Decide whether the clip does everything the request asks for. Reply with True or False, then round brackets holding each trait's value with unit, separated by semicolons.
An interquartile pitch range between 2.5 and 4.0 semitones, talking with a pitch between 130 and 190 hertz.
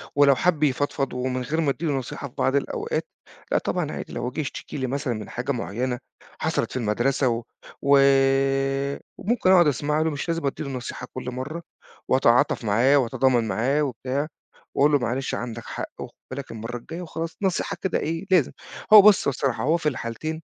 True (3.7 semitones; 135 Hz)